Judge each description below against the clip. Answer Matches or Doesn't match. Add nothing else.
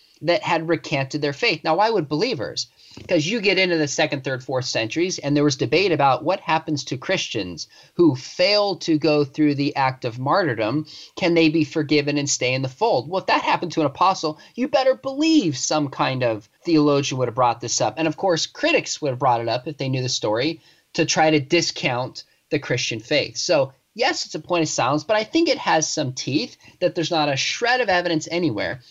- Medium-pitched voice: Matches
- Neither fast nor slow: Doesn't match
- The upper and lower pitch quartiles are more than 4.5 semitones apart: Doesn't match